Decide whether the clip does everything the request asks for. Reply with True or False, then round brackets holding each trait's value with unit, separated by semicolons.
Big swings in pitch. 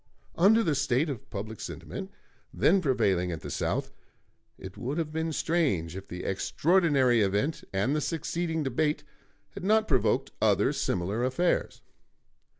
True (8.1 semitones)